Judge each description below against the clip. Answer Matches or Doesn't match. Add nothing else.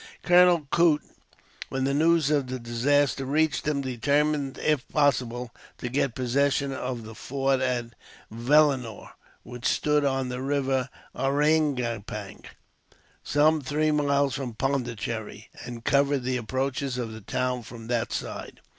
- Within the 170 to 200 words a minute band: Doesn't match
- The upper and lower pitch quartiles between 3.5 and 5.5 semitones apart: Doesn't match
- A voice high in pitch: Doesn't match